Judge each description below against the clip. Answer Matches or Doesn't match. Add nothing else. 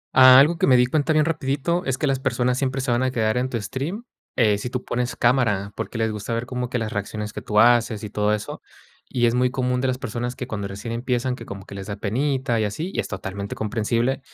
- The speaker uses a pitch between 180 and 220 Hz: Doesn't match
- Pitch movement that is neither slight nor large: Matches